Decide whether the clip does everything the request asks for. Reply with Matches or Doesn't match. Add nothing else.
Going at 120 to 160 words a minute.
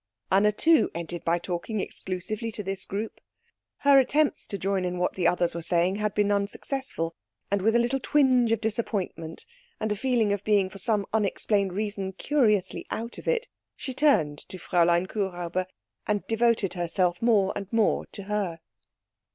Doesn't match